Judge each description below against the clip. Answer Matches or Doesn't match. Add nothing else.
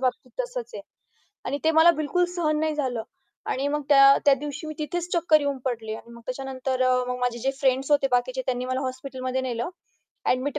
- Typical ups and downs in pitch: Matches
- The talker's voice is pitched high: Matches